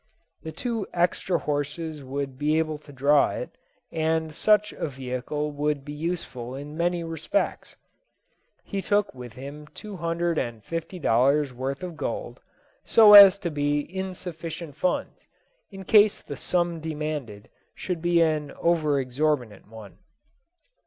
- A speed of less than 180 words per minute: Yes, average, 145 wpm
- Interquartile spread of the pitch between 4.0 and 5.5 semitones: No, average, 3.5 semitones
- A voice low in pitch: No, medium, 155 Hz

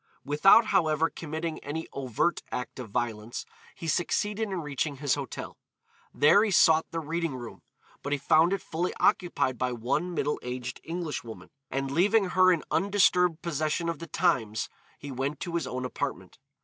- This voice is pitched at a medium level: Yes, medium, 155 Hz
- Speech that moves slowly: No, average, 165 wpm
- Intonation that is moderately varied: Yes, average, 4.7 semitones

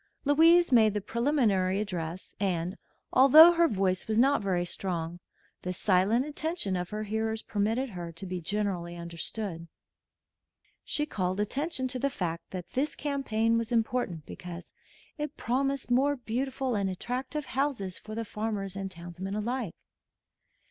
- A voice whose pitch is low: No, high, 215 Hz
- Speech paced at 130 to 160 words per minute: Yes, average, 145 wpm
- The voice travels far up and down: Yes, wide, 6.0 semitones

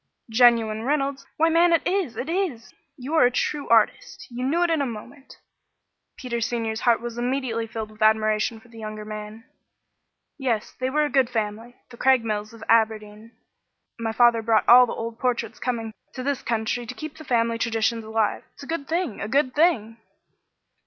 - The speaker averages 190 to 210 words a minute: Yes, average, 195 wpm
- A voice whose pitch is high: Yes, high, 235 Hz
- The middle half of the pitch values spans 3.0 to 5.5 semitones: Yes, average, 3.3 semitones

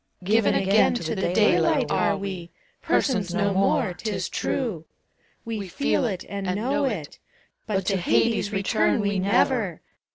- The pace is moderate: Yes, average, 160 wpm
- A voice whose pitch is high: Yes, high, 200 Hz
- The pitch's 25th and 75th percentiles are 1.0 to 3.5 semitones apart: Yes, average, 3.0 semitones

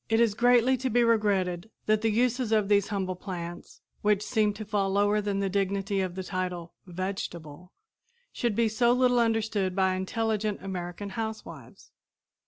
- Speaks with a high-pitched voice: Yes, high, 205 Hz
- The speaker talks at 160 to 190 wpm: Yes, average, 165 wpm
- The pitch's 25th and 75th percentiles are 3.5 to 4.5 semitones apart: No, average, 2.9 semitones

